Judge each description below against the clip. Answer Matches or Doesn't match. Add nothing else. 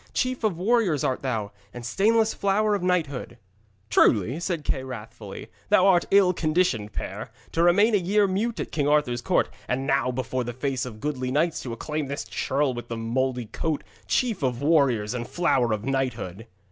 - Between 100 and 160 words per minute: Doesn't match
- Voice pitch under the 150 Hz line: Matches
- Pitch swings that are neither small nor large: Doesn't match